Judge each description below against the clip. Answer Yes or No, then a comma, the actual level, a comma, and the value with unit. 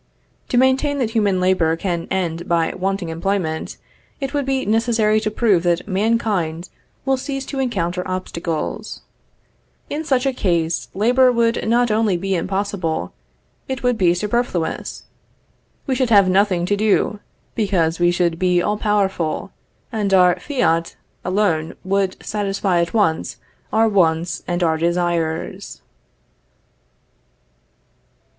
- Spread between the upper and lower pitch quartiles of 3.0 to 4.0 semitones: No, average, 4.7 semitones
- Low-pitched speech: No, high, 195 Hz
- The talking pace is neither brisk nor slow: No, slow, 130 wpm